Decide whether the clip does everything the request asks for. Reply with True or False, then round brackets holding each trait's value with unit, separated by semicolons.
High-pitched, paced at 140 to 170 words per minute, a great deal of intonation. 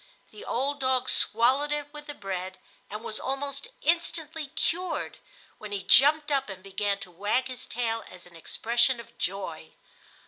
True (250 Hz; 165 wpm; 6.5 semitones)